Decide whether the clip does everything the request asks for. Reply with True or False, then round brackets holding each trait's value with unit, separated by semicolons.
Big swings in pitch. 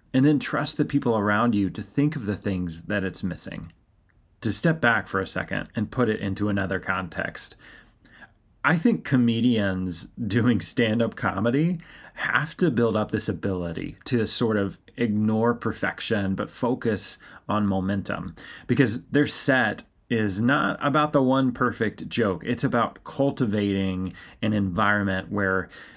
False (4.0 semitones)